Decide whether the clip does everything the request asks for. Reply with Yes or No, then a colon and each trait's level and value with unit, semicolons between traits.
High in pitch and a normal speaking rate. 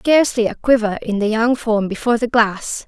No: high, 225 Hz; fast, 210 wpm